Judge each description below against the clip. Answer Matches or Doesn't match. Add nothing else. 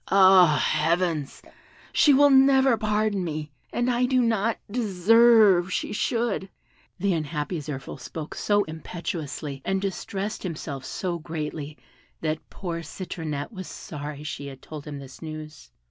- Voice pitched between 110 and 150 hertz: Doesn't match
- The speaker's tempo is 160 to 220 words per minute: Doesn't match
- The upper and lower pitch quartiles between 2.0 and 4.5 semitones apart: Doesn't match